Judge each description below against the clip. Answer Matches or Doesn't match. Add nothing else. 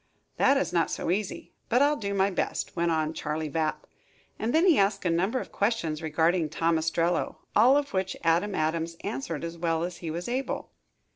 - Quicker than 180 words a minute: Matches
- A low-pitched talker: Doesn't match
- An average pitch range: Matches